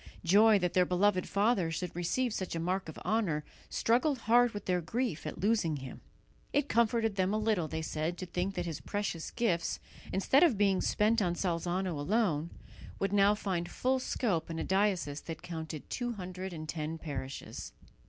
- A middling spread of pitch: Yes, average, 4.4 semitones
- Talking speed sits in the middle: Yes, average, 185 wpm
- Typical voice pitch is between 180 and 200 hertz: Yes, medium, 185 Hz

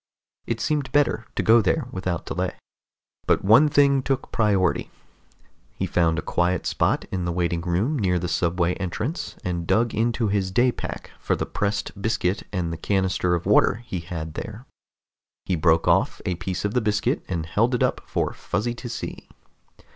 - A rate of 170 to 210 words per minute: Yes, average, 180 wpm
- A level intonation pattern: No, average, 4.9 semitones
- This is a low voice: Yes, low, 100 Hz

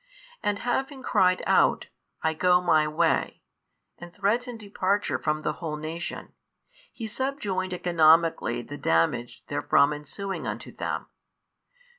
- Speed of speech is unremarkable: No, slow, 120 wpm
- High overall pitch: No, medium, 175 Hz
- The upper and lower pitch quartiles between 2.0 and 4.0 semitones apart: No, average, 4.8 semitones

